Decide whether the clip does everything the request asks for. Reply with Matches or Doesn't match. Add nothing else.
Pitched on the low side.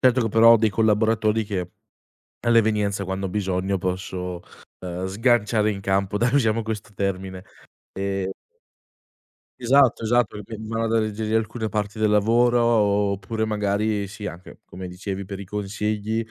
Matches